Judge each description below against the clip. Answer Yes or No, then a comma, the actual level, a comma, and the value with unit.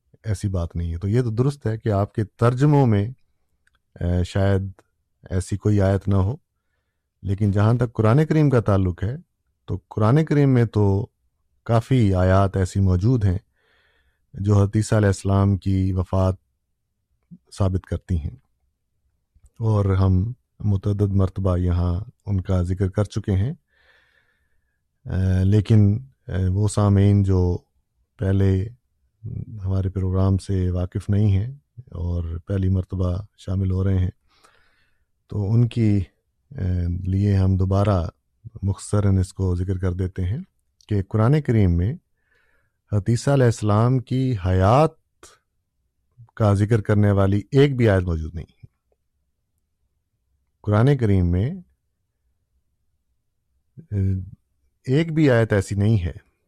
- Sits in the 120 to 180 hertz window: No, low, 100 Hz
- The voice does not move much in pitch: No, average, 3.0 semitones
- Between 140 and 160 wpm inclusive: No, average, 125 wpm